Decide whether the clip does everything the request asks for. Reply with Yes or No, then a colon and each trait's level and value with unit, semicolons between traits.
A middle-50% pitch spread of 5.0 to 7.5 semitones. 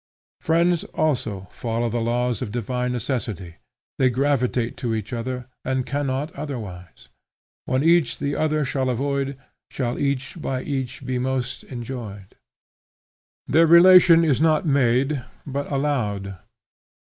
No: average, 3.2 semitones